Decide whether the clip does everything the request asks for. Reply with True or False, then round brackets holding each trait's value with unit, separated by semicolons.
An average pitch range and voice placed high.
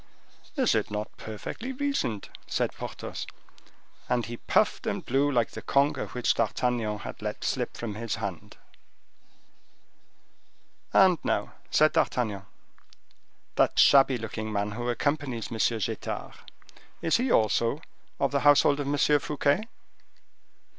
False (4.8 semitones; 120 Hz)